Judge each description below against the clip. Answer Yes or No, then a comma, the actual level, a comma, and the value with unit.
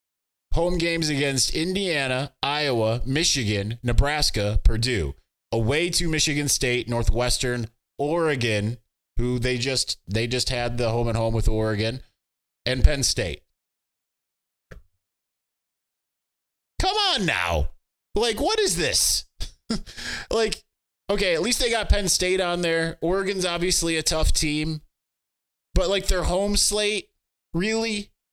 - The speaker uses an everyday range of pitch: No, wide, 7.7 semitones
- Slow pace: Yes, slow, 120 wpm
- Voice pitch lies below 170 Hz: Yes, low, 135 Hz